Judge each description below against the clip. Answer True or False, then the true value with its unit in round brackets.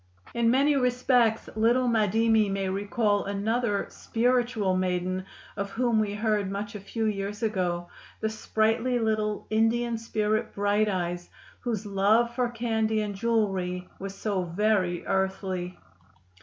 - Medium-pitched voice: False (215 Hz)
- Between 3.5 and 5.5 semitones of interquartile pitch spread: False (2.7 semitones)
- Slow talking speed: True (130 wpm)